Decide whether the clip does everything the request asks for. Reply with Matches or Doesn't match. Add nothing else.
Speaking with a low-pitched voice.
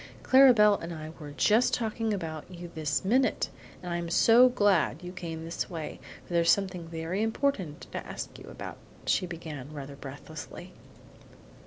Doesn't match